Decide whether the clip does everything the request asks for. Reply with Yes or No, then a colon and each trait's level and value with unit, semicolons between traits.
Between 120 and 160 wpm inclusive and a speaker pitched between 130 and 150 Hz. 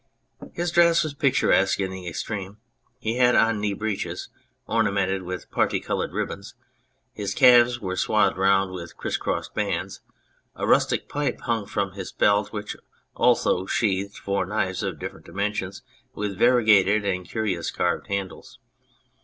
No: average, 145 wpm; low, 100 Hz